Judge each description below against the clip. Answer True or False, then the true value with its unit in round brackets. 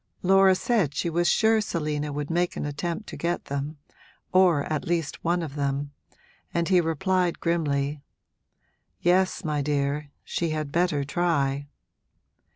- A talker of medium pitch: True (160 Hz)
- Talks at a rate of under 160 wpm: True (145 wpm)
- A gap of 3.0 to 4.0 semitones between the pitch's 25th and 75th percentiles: True (3.4 semitones)